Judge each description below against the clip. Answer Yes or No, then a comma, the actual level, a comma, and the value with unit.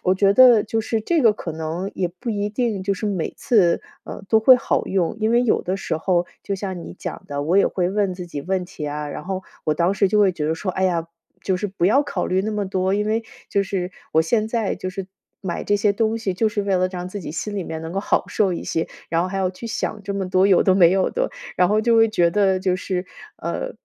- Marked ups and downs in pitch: No, average, 2.7 semitones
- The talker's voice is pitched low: No, high, 190 Hz